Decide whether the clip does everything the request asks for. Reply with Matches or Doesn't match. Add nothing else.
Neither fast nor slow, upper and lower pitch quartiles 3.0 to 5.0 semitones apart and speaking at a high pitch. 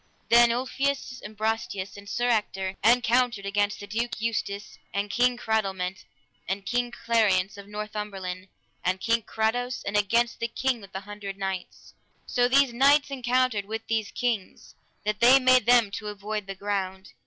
Matches